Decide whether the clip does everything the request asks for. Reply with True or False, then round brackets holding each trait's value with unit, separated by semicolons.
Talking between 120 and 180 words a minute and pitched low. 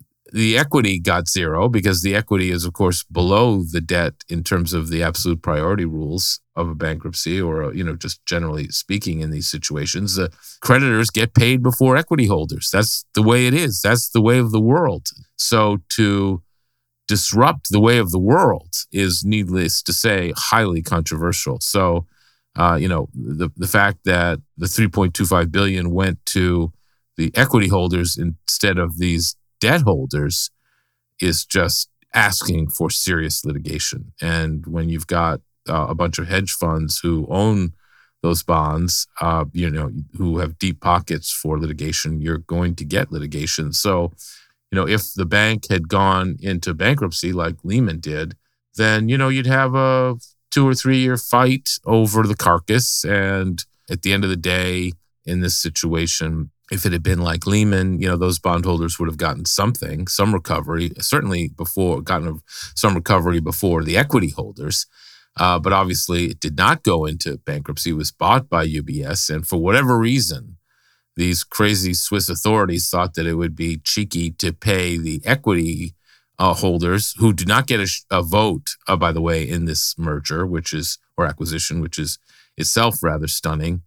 True (170 wpm; 90 Hz)